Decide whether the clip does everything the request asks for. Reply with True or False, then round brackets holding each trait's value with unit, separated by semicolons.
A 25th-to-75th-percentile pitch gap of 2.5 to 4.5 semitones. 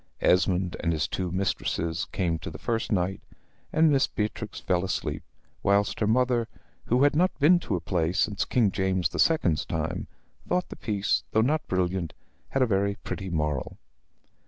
False (5.1 semitones)